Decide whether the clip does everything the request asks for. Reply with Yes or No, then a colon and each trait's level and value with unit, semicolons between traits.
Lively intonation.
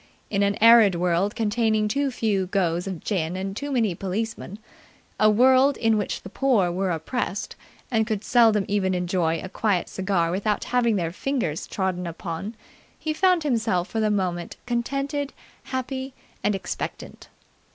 No: average, 4.4 semitones